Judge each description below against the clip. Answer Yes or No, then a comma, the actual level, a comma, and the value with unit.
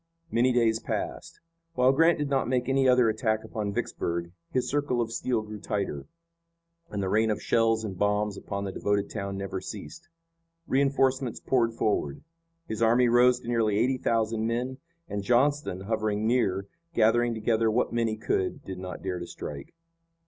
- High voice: No, low, 110 Hz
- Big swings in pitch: No, average, 3.4 semitones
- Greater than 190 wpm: No, average, 170 wpm